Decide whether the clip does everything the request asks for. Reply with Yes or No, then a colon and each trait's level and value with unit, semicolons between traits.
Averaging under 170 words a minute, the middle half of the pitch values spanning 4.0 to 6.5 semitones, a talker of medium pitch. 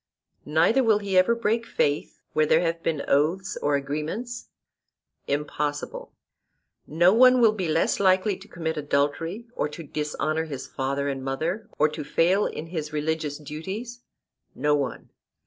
Yes: average, 150 wpm; average, 4.7 semitones; medium, 160 Hz